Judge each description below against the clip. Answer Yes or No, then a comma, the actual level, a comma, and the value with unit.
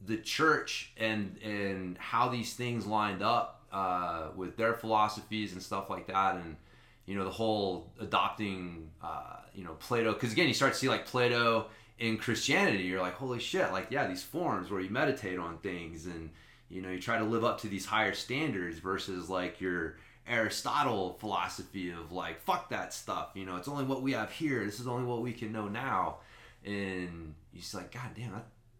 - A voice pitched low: Yes, low, 105 Hz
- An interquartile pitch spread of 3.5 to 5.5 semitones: Yes, average, 4.0 semitones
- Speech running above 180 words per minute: Yes, average, 200 wpm